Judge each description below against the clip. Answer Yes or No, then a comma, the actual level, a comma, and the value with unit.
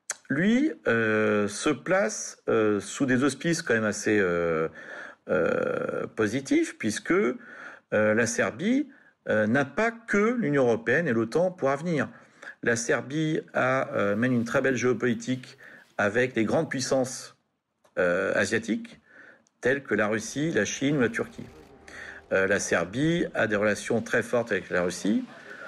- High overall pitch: No, medium, 140 Hz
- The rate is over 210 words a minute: No, slow, 145 wpm